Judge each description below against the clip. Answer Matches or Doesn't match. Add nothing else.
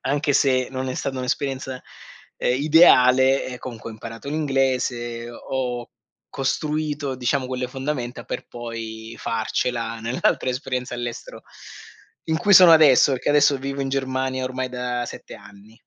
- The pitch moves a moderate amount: Doesn't match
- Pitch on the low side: Matches